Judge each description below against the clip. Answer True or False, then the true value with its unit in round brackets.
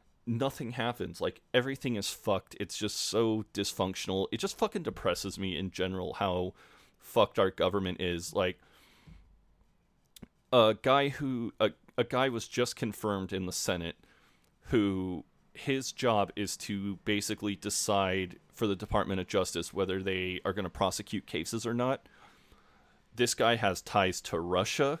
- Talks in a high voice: False (105 Hz)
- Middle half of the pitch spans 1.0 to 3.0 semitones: False (4.1 semitones)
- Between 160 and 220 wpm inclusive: False (150 wpm)